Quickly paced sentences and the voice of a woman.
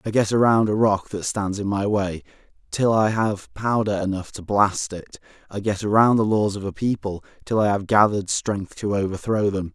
No: fast, 210 wpm; male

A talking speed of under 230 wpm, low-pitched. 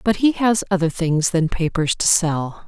No: average, 200 wpm; medium, 175 Hz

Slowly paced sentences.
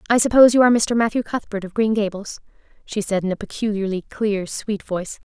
No: fast, 205 wpm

